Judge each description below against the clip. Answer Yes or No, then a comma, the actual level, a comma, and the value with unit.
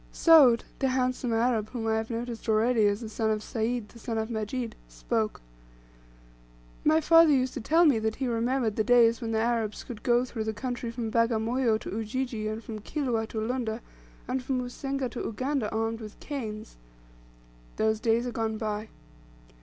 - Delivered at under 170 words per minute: No, average, 185 wpm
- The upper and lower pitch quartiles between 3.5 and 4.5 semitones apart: No, narrow, 2.5 semitones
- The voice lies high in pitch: Yes, high, 230 Hz